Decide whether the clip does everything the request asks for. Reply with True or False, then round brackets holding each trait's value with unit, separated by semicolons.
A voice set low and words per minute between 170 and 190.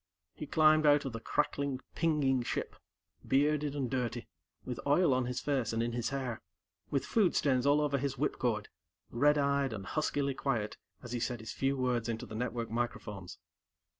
True (130 Hz; 180 wpm)